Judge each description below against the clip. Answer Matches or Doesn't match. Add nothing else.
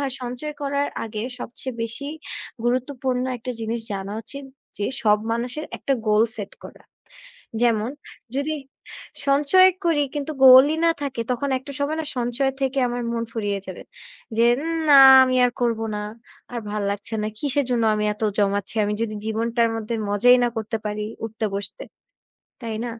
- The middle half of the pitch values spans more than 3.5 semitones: Matches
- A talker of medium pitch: Doesn't match